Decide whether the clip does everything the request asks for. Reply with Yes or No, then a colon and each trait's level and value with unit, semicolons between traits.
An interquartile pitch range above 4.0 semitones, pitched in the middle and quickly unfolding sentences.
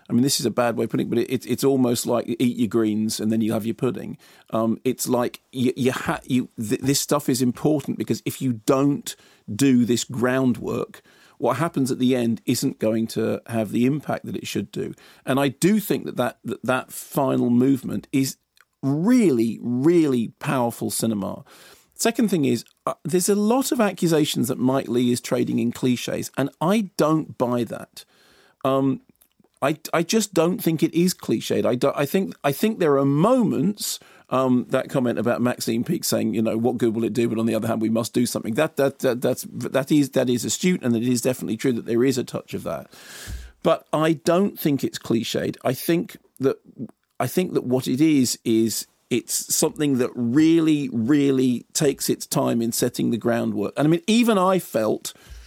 No: average, 4.7 semitones; low, 130 Hz; fast, 210 wpm